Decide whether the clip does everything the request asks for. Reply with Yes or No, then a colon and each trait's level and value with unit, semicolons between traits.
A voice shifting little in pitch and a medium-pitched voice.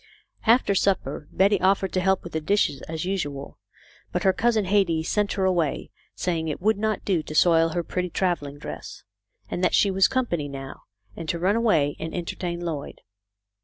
No: average, 3.6 semitones; medium, 180 Hz